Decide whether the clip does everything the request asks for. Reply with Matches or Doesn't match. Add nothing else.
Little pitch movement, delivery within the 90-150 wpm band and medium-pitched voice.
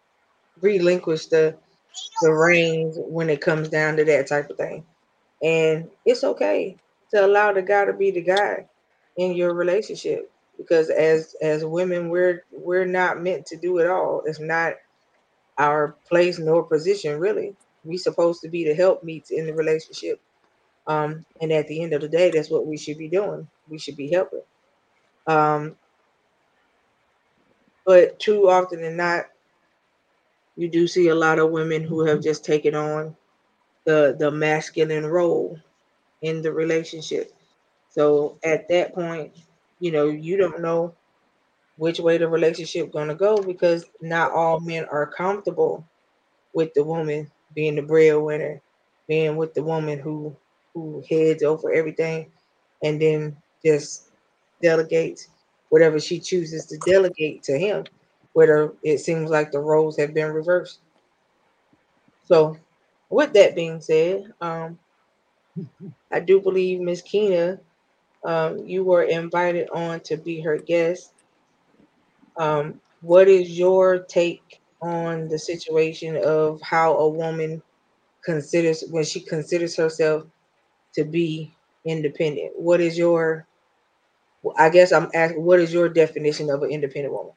Matches